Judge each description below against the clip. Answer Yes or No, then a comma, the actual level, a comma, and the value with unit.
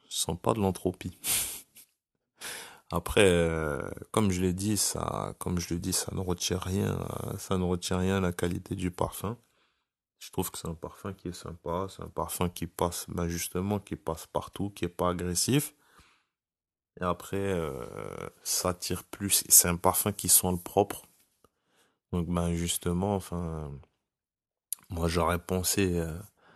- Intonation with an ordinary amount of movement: No, narrow, 2.1 semitones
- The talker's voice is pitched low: Yes, very low, 90 Hz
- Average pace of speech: Yes, average, 165 wpm